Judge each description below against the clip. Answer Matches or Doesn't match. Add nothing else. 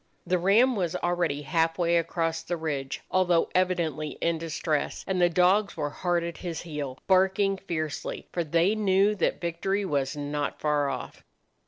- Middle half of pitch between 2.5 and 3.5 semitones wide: Matches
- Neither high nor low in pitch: Matches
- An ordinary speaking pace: Matches